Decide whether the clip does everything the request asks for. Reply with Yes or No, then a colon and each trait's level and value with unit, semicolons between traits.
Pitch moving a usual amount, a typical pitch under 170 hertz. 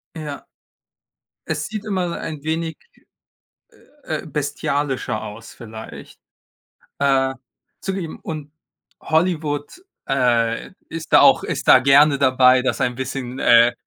Yes: average, 3.8 semitones; medium, 140 Hz